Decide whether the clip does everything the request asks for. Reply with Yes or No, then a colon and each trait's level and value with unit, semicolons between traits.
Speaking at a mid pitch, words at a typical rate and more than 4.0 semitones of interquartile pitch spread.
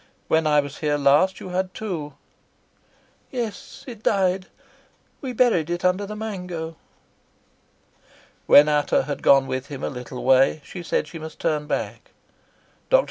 Yes: medium, 160 Hz; average, 150 wpm; average, 4.7 semitones